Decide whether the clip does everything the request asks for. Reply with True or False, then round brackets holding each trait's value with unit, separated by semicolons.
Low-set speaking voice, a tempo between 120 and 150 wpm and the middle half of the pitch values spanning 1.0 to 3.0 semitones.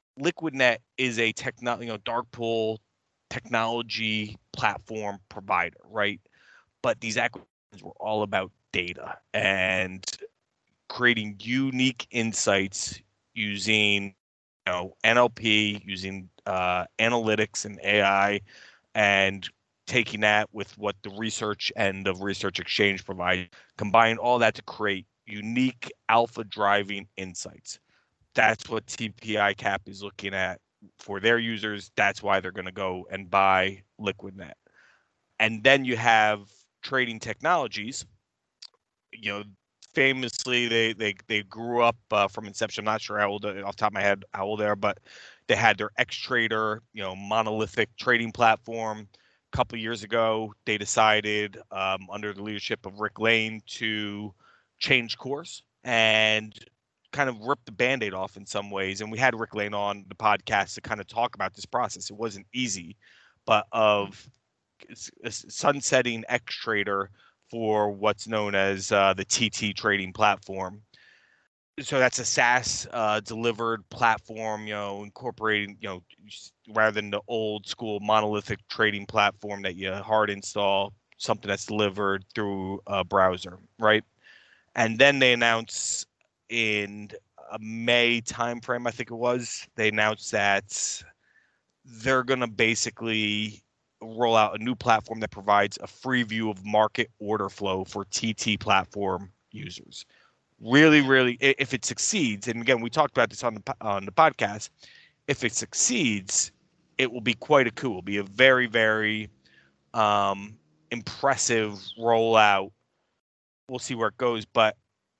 True (110 Hz; 145 wpm; 2.5 semitones)